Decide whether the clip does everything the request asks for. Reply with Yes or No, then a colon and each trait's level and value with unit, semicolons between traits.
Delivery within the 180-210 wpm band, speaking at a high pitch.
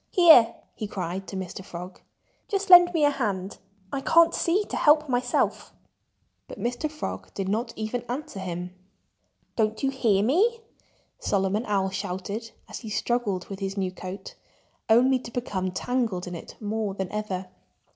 No: average, 160 wpm; high, 215 Hz